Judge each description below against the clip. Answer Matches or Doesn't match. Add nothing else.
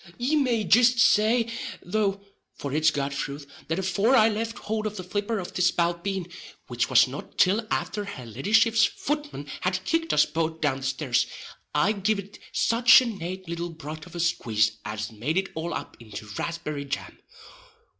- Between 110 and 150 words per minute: Doesn't match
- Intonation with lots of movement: Matches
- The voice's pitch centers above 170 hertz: Matches